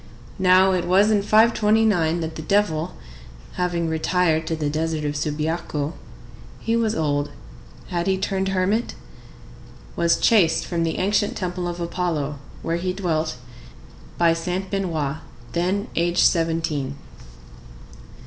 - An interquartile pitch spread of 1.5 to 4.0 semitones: Yes, average, 3.0 semitones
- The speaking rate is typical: No, slow, 120 wpm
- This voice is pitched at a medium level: Yes, medium, 170 Hz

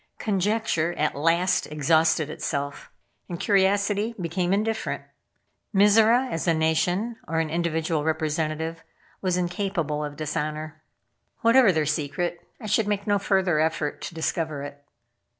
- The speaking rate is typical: No, slow, 130 wpm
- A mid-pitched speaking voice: Yes, medium, 165 Hz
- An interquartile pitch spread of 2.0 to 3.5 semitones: No, average, 4.2 semitones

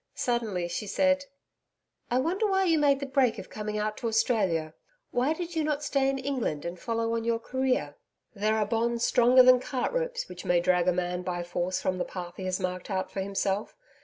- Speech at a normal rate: No, fast, 215 wpm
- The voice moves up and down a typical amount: No, wide, 6.5 semitones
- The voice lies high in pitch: Yes, high, 230 Hz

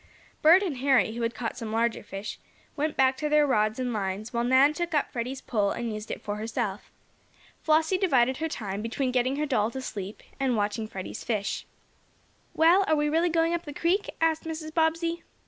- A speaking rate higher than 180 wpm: Yes, average, 200 wpm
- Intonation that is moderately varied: No, wide, 6.1 semitones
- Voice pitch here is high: Yes, very high, 260 Hz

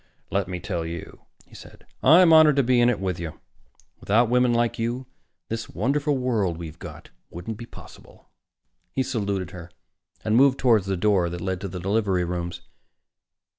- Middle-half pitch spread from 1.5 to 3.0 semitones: No, wide, 5.6 semitones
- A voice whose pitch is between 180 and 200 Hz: No, low, 105 Hz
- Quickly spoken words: No, average, 175 wpm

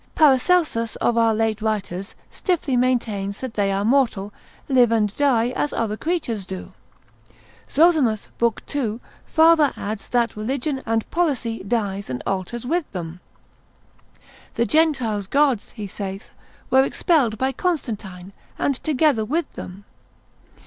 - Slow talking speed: Yes, slow, 130 wpm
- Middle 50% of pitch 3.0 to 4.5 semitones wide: No, average, 5.3 semitones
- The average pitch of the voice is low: No, high, 230 Hz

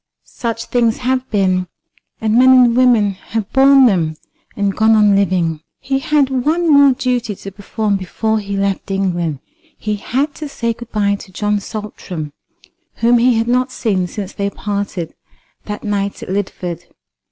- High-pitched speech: Yes, high, 210 Hz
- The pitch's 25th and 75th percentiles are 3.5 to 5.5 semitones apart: Yes, average, 4.0 semitones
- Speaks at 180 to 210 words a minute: No, average, 165 wpm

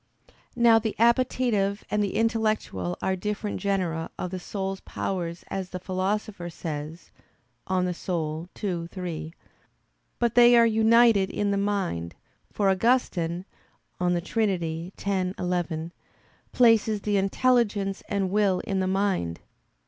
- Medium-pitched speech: No, high, 195 Hz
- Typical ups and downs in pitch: Yes, average, 3.3 semitones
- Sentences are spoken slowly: Yes, slow, 125 wpm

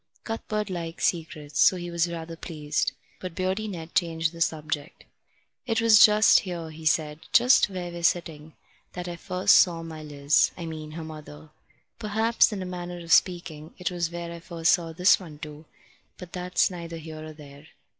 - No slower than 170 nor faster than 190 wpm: Yes, average, 185 wpm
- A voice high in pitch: No, medium, 170 Hz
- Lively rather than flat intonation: No, narrow, 2.4 semitones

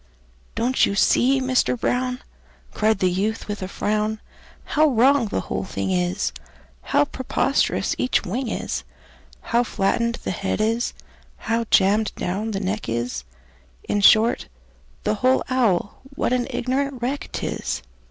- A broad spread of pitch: No, average, 4.4 semitones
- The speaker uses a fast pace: No, average, 145 wpm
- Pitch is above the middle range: Yes, high, 220 Hz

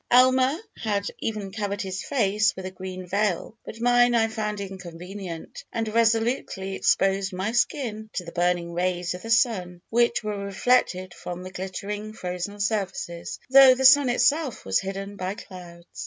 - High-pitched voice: Yes, high, 200 Hz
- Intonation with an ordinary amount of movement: Yes, average, 3.7 semitones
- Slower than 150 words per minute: No, average, 160 wpm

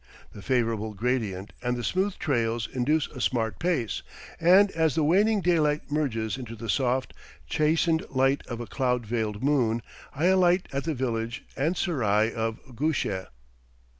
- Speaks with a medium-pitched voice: No, low, 130 Hz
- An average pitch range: No, wide, 5.7 semitones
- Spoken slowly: No, average, 155 wpm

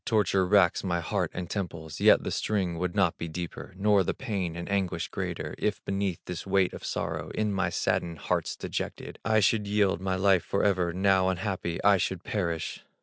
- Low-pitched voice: Yes, very low, 95 Hz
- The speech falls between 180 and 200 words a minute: Yes, average, 190 wpm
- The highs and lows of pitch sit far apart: No, narrow, 2.5 semitones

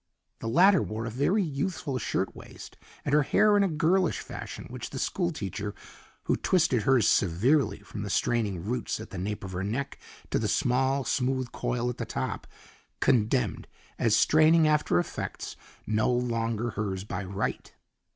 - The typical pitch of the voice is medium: No, low, 125 Hz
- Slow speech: No, average, 170 wpm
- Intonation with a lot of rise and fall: Yes, wide, 5.9 semitones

